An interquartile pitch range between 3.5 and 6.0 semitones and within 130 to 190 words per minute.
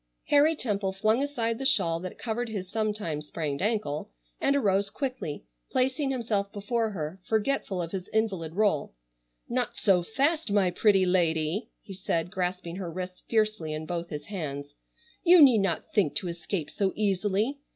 Yes: average, 4.7 semitones; average, 160 wpm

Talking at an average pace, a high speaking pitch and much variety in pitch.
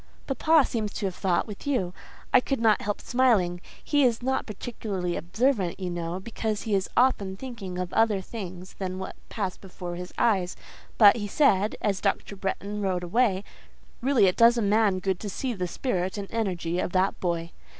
No: average, 190 wpm; high, 200 Hz; average, 3.9 semitones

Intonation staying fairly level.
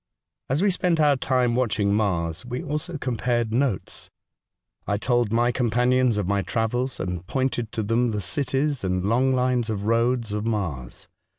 No: average, 3.7 semitones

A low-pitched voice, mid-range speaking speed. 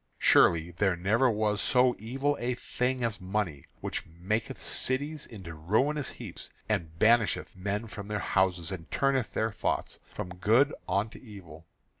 Yes: low, 105 Hz; average, 150 wpm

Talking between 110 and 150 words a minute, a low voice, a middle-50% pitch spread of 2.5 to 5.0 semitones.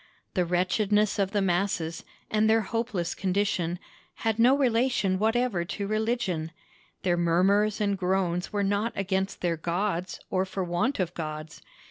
No: average, 145 wpm; high, 195 Hz; average, 3.3 semitones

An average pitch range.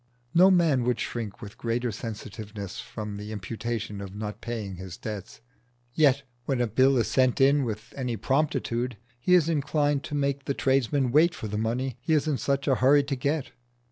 Yes: average, 4.4 semitones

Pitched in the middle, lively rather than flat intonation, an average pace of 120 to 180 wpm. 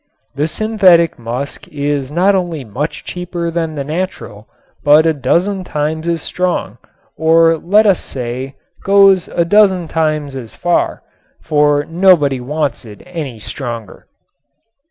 No: medium, 160 Hz; average, 4.0 semitones; slow, 135 wpm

